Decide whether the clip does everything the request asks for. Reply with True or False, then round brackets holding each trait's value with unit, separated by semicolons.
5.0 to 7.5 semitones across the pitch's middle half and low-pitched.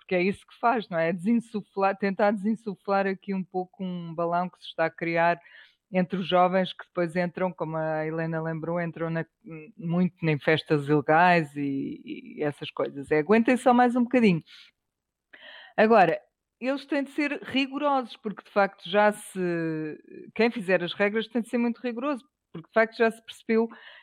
False (5.4 semitones; 190 Hz)